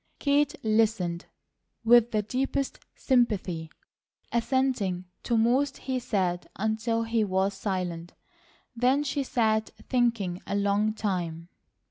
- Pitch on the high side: Yes, high, 220 Hz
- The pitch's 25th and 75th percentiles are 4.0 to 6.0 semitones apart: Yes, average, 4.3 semitones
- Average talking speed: No, slow, 110 wpm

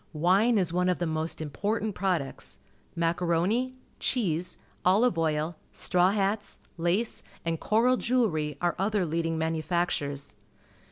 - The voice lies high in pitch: No, medium, 175 Hz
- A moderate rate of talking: No, slow, 120 wpm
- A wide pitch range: No, average, 4.2 semitones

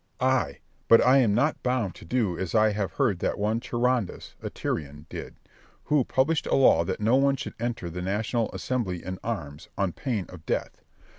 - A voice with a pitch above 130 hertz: No, low, 110 Hz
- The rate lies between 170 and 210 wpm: Yes, average, 200 wpm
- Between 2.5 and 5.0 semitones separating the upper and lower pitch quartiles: No, wide, 5.6 semitones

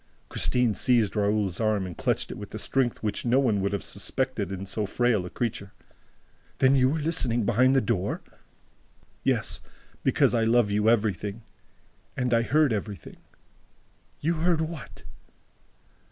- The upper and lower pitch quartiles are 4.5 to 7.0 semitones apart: No, average, 4.1 semitones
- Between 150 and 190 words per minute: Yes, average, 160 wpm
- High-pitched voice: No, low, 115 Hz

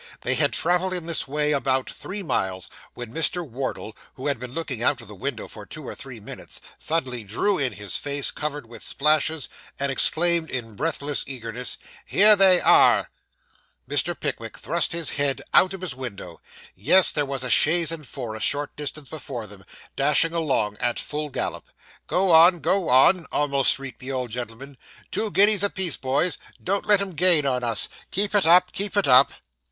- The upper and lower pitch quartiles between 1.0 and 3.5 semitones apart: No, average, 5.2 semitones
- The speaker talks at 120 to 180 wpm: No, average, 190 wpm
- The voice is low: No, medium, 145 Hz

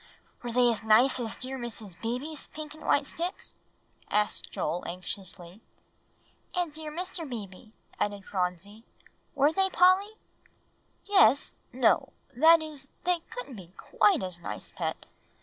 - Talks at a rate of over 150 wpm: No, slow, 135 wpm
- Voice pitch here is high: Yes, very high, 250 Hz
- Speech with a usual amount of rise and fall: No, wide, 7.4 semitones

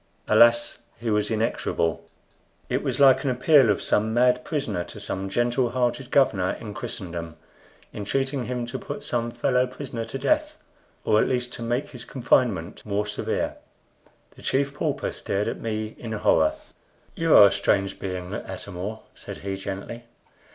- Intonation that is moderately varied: Yes, average, 4.0 semitones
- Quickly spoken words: No, average, 165 wpm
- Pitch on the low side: Yes, low, 115 Hz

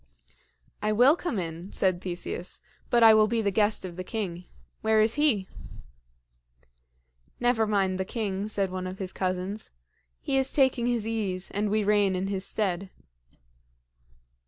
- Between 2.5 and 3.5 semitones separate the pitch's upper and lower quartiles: Yes, average, 3.1 semitones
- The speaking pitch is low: No, high, 205 Hz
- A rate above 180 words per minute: No, average, 160 wpm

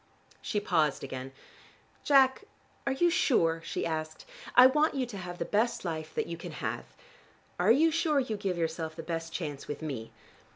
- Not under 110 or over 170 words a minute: No, average, 180 wpm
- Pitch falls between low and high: Yes, medium, 175 Hz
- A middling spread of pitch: No, wide, 8.4 semitones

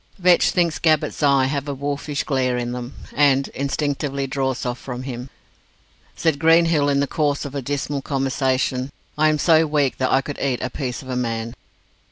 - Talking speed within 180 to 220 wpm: Yes, average, 190 wpm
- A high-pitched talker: No, medium, 140 Hz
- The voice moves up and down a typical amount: No, narrow, 2.2 semitones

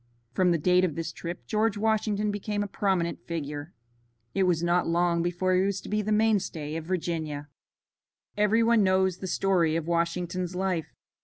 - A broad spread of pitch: No, average, 3.1 semitones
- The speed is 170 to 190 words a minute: Yes, average, 175 wpm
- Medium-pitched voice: Yes, medium, 180 Hz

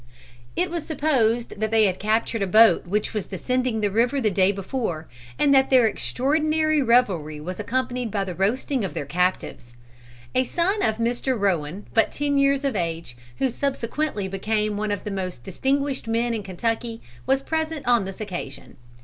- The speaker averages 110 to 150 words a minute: No, average, 175 wpm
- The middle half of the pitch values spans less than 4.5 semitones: No, wide, 5.4 semitones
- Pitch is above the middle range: Yes, high, 225 Hz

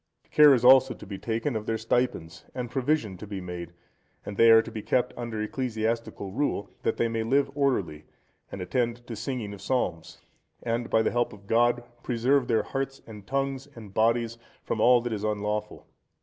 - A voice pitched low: Yes, low, 115 Hz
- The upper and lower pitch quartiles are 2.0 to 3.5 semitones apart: Yes, average, 3.0 semitones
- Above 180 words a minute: Yes, average, 190 wpm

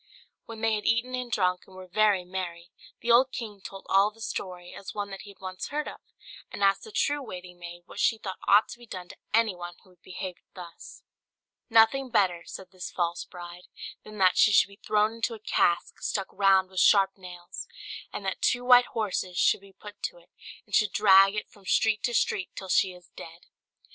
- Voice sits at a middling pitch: No, high, 195 Hz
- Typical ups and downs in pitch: Yes, average, 3.3 semitones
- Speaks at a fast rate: Yes, fast, 215 wpm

